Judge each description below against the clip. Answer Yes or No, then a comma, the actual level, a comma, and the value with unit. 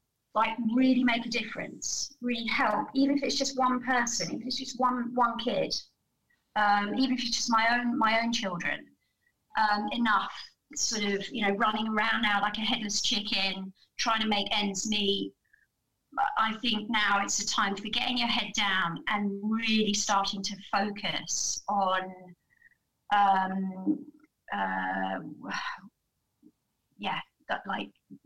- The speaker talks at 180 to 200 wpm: No, average, 145 wpm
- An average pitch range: Yes, average, 3.4 semitones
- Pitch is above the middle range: Yes, high, 220 Hz